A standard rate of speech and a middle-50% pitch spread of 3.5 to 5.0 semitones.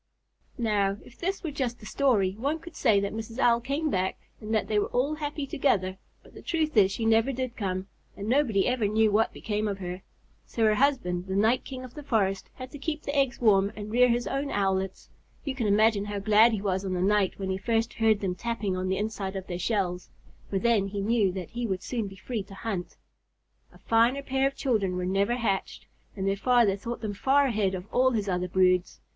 No: fast, 230 wpm; average, 4.2 semitones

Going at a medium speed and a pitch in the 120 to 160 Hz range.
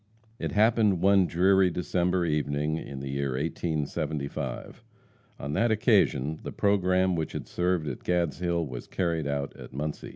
No: average, 150 wpm; very low, 85 Hz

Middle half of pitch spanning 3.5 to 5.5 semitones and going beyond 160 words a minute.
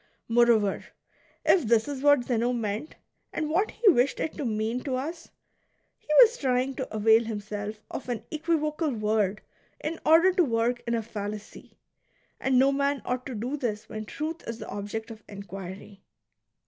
Yes: average, 5.1 semitones; average, 170 wpm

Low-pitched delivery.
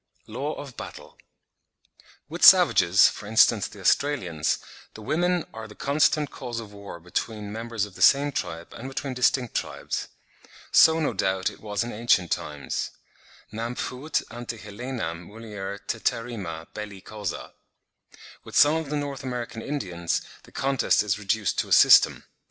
Yes: low, 115 Hz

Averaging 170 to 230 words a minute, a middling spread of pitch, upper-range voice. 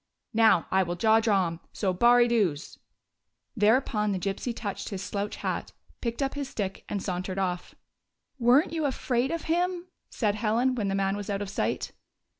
Yes: average, 195 wpm; average, 4.0 semitones; high, 210 Hz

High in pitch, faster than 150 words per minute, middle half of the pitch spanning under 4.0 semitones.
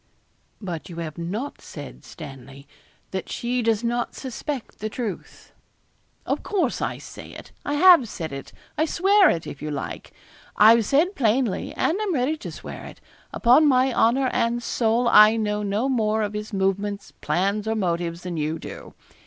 No: high, 220 Hz; average, 170 wpm; wide, 5.4 semitones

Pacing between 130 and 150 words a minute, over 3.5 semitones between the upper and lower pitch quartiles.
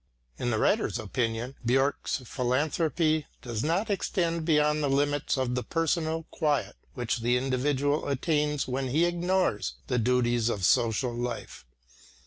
Yes: slow, 135 wpm; average, 4.4 semitones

